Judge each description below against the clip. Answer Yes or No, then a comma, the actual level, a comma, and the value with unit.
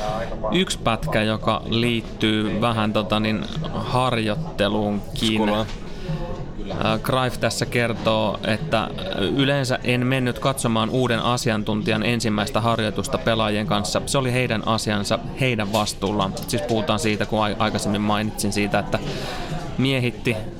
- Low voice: Yes, low, 110 Hz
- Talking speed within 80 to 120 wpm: Yes, average, 110 wpm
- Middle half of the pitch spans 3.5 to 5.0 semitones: No, narrow, 2.5 semitones